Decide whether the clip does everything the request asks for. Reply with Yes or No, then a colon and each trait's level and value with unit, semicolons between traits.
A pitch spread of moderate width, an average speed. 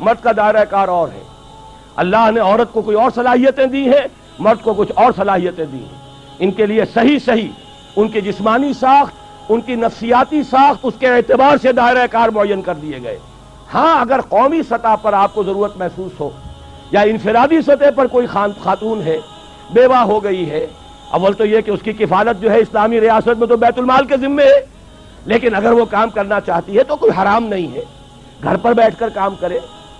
No: average, 3.9 semitones; fast, 205 wpm